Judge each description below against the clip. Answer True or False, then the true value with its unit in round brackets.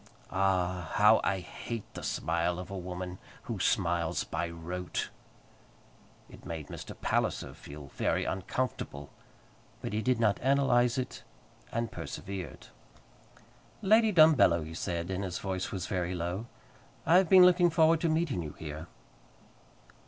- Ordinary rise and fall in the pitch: False (6.8 semitones)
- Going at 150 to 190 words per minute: False (140 wpm)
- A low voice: True (95 Hz)